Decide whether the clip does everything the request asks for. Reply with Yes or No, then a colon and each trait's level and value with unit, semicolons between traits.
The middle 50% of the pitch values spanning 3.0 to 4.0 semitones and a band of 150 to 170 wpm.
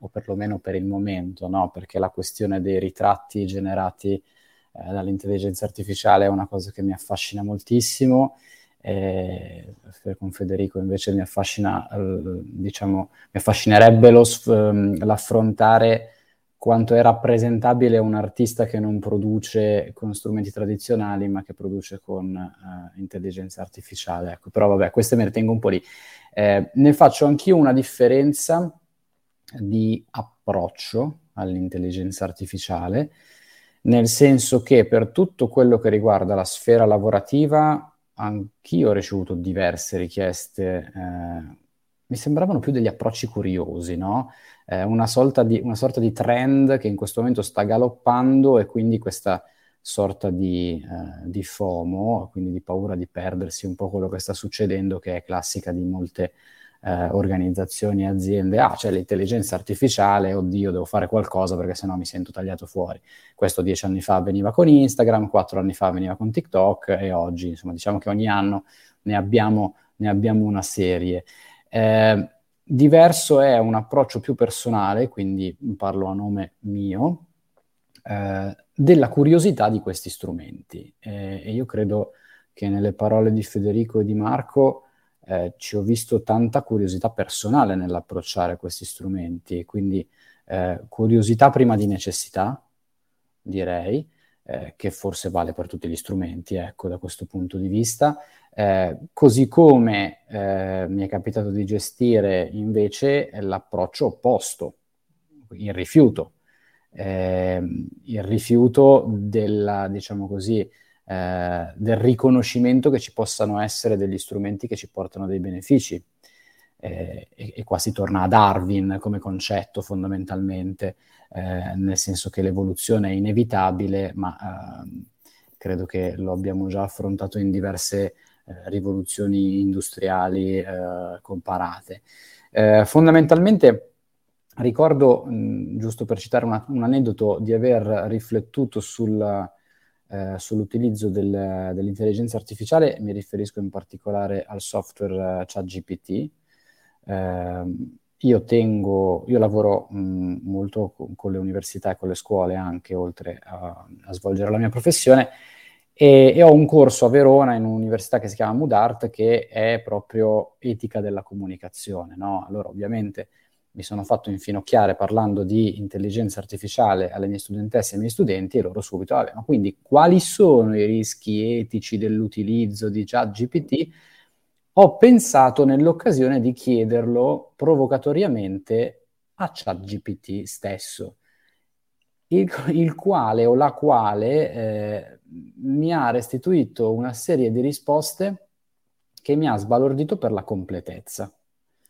No: average, 3.4 semitones; average, 135 wpm